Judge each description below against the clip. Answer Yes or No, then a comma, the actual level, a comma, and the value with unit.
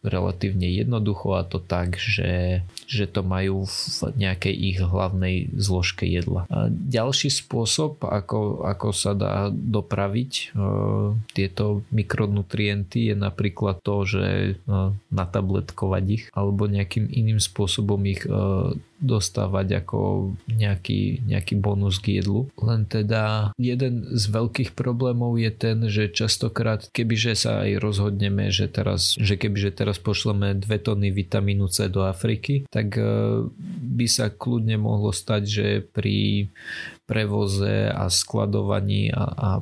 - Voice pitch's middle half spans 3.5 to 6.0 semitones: No, narrow, 2.4 semitones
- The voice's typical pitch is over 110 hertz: No, low, 105 Hz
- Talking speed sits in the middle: Yes, average, 130 wpm